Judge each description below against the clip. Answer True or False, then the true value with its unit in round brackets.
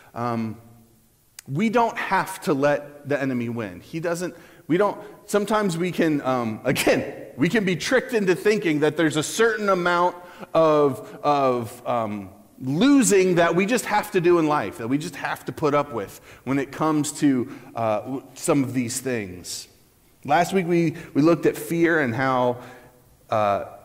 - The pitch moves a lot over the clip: True (6.2 semitones)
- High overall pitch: False (145 Hz)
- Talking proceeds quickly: False (170 wpm)